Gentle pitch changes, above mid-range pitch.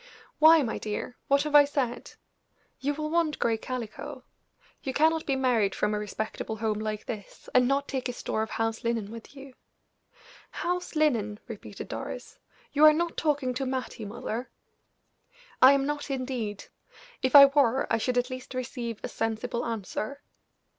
No: average, 4.0 semitones; very high, 255 Hz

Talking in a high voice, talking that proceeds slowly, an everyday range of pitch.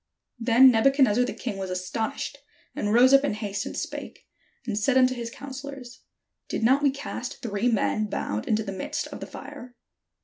No: high, 240 Hz; average, 190 wpm; average, 4.0 semitones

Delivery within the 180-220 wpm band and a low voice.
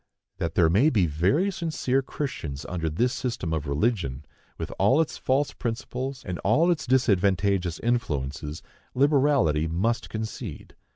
No: slow, 135 wpm; low, 110 Hz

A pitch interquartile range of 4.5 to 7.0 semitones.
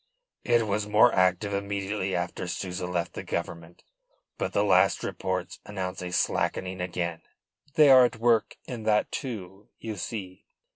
No: average, 3.1 semitones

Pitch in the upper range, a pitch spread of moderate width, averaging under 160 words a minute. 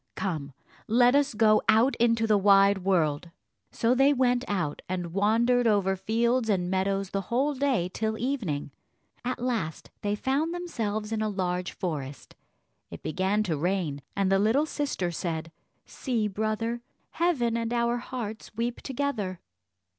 Yes: high, 215 Hz; average, 4.4 semitones; average, 150 wpm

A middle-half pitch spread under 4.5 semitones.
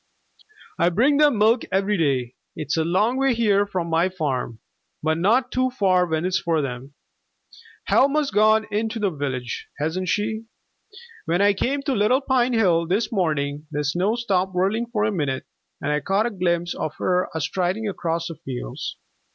No: wide, 5.4 semitones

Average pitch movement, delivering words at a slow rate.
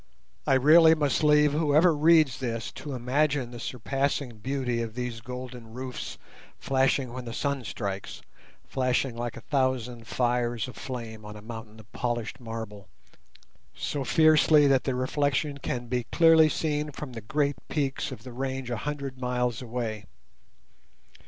No: average, 3.3 semitones; average, 145 wpm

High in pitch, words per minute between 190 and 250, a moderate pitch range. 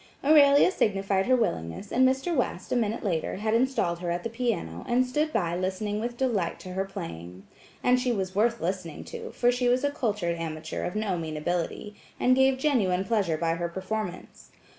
No: high, 205 Hz; average, 195 wpm; wide, 6.2 semitones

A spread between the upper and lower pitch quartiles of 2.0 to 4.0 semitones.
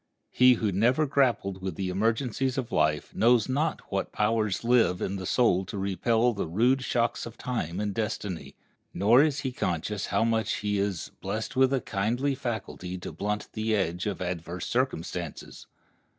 No: average, 4.6 semitones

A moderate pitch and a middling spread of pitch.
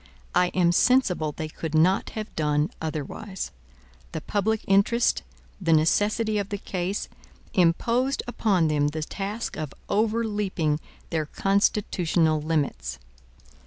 Yes: medium, 180 Hz; average, 5.0 semitones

